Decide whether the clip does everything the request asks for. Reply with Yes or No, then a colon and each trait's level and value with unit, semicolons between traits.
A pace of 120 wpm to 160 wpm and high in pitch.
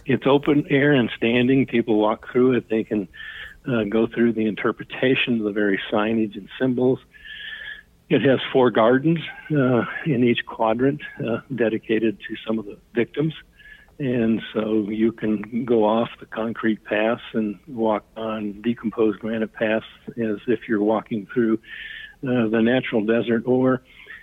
No: average, 155 wpm; low, 115 Hz